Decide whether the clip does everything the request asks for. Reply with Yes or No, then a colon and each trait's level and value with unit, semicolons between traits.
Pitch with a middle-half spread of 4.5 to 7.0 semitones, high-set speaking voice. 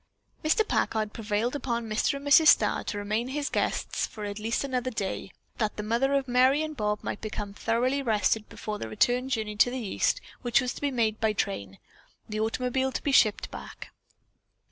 No: average, 3.7 semitones; high, 230 Hz